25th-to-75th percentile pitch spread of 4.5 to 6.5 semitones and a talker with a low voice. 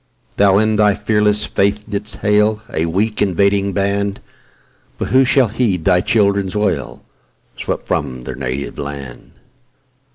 No: narrow, 2.6 semitones; low, 100 Hz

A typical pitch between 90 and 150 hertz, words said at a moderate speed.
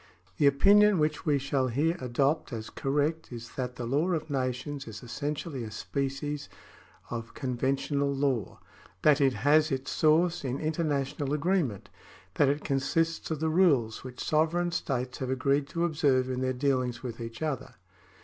Yes: medium, 140 Hz; average, 170 wpm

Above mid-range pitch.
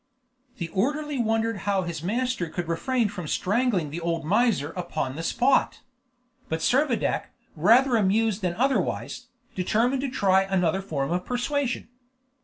Yes: high, 200 Hz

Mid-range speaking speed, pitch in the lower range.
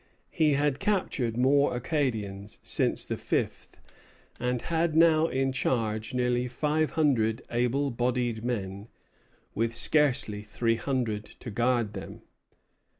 No: slow, 120 wpm; low, 125 Hz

